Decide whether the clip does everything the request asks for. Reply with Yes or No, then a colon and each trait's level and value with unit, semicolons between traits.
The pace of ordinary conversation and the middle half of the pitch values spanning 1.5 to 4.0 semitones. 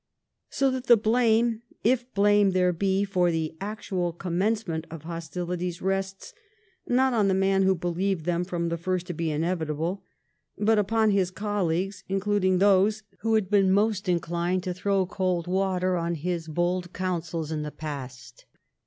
Yes: average, 160 wpm; average, 3.0 semitones